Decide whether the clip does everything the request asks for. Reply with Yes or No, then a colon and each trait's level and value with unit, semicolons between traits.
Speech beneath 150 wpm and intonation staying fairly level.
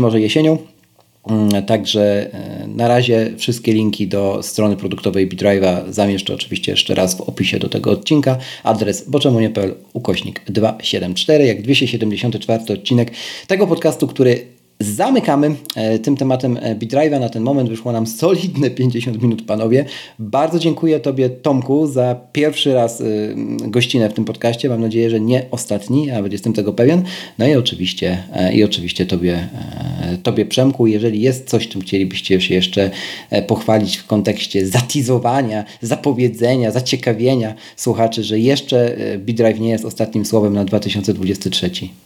No: average, 135 wpm; average, 4.0 semitones